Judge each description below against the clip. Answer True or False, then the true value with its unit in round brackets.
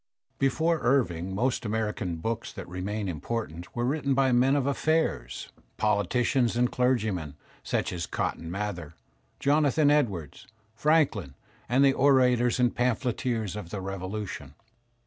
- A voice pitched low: True (115 Hz)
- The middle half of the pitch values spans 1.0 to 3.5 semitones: False (5.6 semitones)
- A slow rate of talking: True (125 wpm)